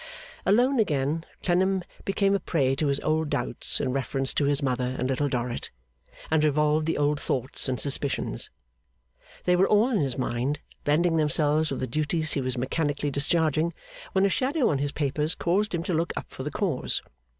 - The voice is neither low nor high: Yes, medium, 150 Hz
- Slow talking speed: No, average, 185 wpm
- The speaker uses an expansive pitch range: No, average, 4.0 semitones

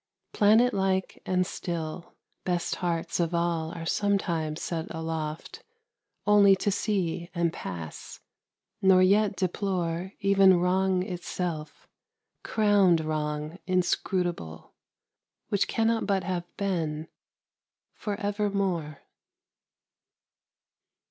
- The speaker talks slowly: Yes, slow, 95 wpm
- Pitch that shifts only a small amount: No, average, 3.2 semitones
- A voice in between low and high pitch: Yes, medium, 180 Hz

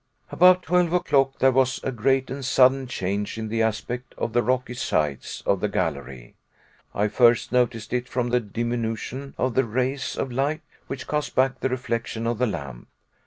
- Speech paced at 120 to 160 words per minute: No, average, 180 wpm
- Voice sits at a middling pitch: No, low, 125 Hz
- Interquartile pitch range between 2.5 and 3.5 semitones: Yes, average, 3.0 semitones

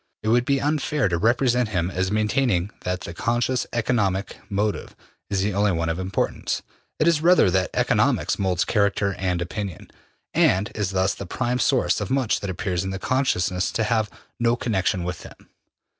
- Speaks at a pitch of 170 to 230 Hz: No, low, 100 Hz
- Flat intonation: No, average, 4.3 semitones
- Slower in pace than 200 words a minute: Yes, average, 175 wpm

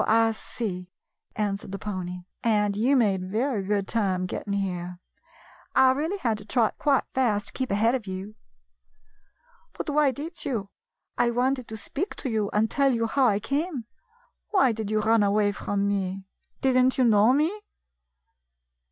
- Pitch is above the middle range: Yes, high, 220 Hz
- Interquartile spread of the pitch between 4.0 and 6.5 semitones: Yes, average, 4.5 semitones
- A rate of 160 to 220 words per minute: Yes, average, 175 wpm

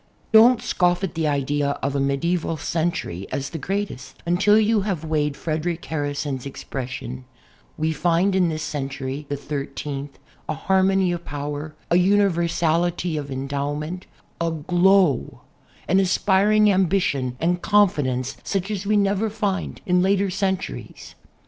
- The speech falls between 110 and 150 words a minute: Yes, average, 140 wpm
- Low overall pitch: No, medium, 165 Hz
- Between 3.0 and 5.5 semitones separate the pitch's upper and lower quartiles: Yes, average, 4.9 semitones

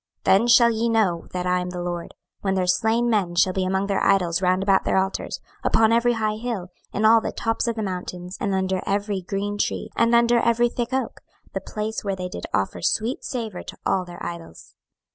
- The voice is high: Yes, high, 195 Hz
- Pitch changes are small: No, average, 3.8 semitones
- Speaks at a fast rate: Yes, fast, 220 wpm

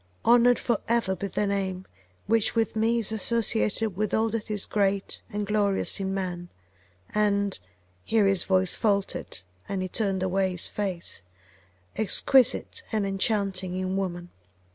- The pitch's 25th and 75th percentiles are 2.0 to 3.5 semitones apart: Yes, narrow, 2.5 semitones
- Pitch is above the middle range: Yes, high, 200 Hz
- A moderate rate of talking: Yes, average, 145 wpm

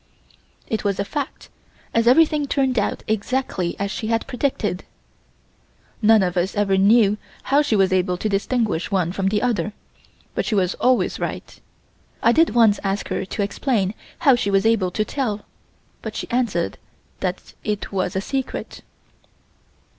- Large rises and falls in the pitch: No, average, 3.9 semitones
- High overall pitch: Yes, high, 210 Hz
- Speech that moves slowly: No, average, 160 wpm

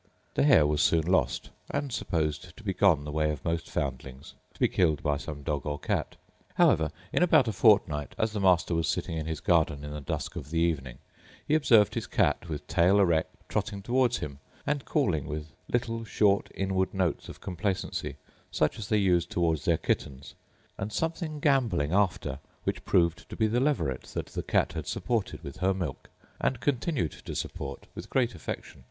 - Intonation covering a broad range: Yes, wide, 6.1 semitones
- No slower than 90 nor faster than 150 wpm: No, average, 195 wpm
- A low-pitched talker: Yes, very low, 90 Hz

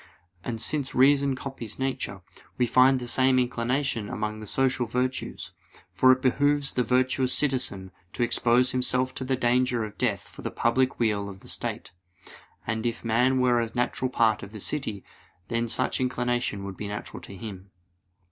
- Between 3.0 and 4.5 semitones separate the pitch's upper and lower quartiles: No, narrow, 2.6 semitones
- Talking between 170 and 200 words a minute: Yes, average, 175 wpm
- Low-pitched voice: Yes, low, 125 Hz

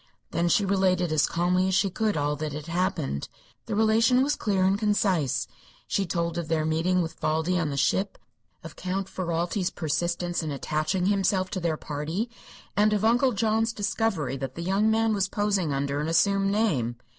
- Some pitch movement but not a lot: Yes, average, 4.4 semitones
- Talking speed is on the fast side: No, average, 185 wpm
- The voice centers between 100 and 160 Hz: No, medium, 185 Hz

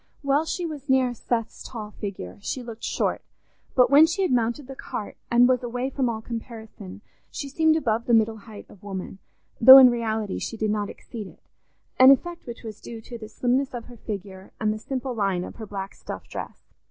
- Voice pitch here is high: Yes, high, 235 Hz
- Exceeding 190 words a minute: Yes, fast, 205 wpm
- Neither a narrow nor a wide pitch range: Yes, average, 3.4 semitones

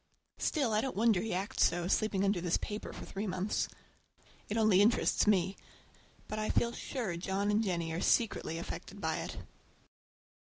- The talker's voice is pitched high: Yes, high, 200 Hz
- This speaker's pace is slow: No, average, 170 wpm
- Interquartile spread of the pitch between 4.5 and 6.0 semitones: No, average, 3.2 semitones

